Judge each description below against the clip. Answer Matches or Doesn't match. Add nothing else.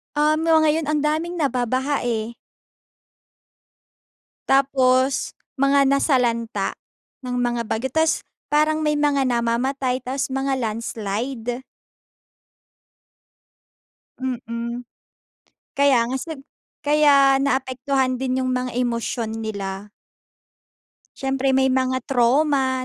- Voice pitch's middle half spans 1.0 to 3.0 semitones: Matches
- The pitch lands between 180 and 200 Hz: Doesn't match